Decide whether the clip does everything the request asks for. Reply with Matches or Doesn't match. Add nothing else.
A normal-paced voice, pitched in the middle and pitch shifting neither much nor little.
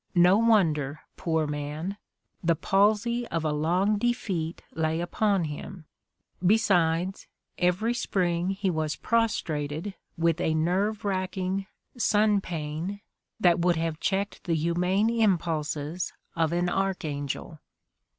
Doesn't match